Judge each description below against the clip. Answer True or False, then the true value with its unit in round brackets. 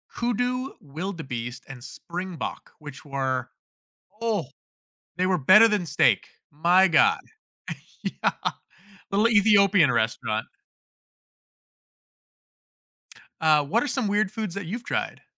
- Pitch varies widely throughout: True (6.6 semitones)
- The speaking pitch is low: False (185 Hz)